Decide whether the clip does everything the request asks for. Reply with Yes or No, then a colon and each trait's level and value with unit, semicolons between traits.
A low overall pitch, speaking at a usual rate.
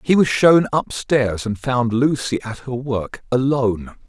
Yes: low, 125 Hz; average, 175 wpm